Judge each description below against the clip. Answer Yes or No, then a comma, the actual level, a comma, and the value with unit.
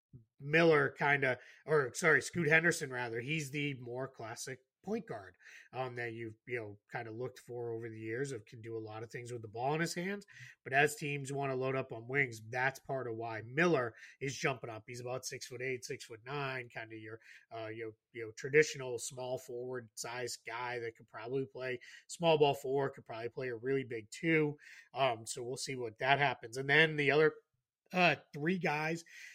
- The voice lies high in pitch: No, low, 130 Hz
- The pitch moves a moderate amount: Yes, average, 3.6 semitones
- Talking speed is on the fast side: Yes, fast, 210 wpm